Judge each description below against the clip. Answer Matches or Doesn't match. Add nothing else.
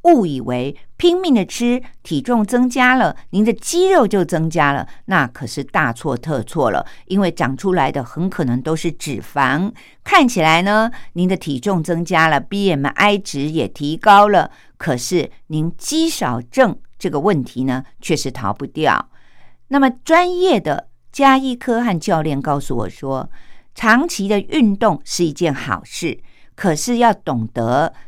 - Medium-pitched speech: Matches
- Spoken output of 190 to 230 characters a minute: Matches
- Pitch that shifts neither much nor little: Doesn't match